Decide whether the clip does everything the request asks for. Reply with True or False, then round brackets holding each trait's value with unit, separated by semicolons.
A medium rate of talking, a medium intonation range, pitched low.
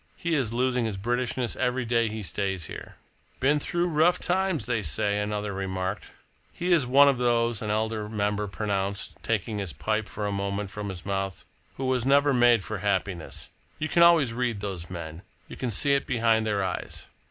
True (190 wpm; 4.2 semitones; 110 Hz)